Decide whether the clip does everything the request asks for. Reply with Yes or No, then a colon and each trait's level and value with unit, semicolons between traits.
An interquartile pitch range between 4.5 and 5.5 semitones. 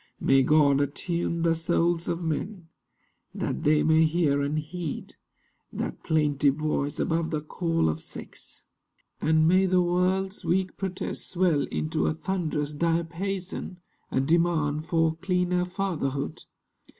No: average, 3.0 semitones